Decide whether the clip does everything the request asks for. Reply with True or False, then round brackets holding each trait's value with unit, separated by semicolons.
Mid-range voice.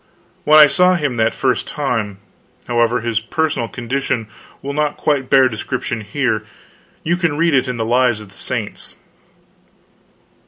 False (130 Hz)